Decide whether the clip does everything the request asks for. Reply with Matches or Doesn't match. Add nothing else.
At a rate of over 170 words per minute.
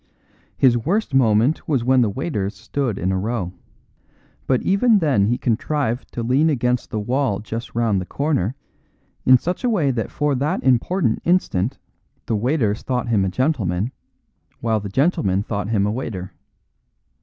Doesn't match